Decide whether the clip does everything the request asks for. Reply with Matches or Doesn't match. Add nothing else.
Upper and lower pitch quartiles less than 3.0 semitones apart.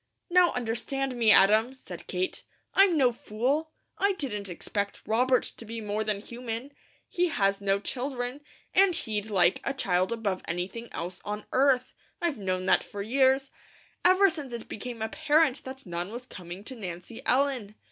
Doesn't match